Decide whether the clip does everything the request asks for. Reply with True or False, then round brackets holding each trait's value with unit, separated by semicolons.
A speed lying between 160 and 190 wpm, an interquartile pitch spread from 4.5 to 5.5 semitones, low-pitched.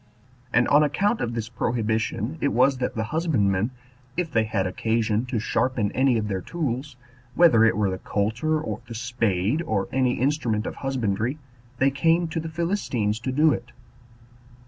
True (170 wpm; 5.0 semitones; 120 Hz)